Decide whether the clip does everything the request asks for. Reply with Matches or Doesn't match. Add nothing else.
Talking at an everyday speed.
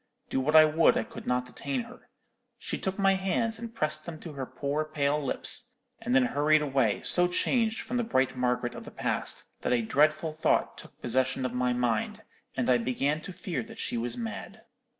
Doesn't match